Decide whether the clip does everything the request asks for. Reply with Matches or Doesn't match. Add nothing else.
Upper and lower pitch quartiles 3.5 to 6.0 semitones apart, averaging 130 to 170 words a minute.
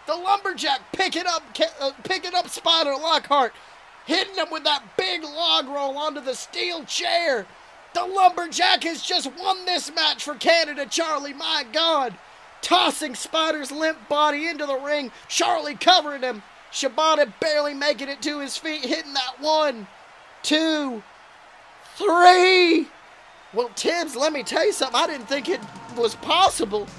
Doesn't match